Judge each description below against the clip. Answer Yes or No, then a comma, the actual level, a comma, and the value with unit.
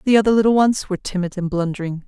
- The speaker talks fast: Yes, fast, 230 wpm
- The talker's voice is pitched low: No, high, 195 Hz